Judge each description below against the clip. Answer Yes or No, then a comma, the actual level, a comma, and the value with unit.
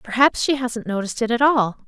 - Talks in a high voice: Yes, high, 240 Hz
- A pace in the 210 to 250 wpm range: Yes, fast, 225 wpm